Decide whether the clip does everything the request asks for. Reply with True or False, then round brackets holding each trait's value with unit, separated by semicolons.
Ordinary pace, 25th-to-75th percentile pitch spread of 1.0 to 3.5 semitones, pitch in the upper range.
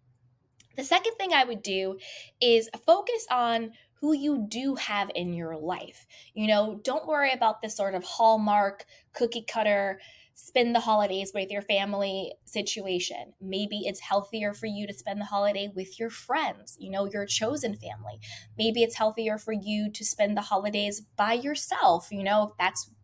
True (170 wpm; 2.7 semitones; 205 Hz)